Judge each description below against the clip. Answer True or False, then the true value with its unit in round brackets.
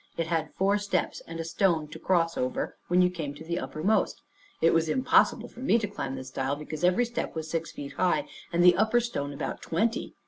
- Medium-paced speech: False (220 wpm)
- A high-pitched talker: False (165 Hz)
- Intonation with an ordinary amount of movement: True (4.2 semitones)